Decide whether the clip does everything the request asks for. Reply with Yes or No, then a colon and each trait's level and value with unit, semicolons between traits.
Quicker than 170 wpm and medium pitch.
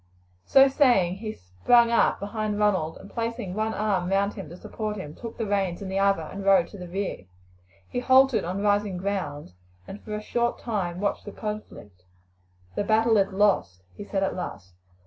No: average, 190 wpm; high, 200 Hz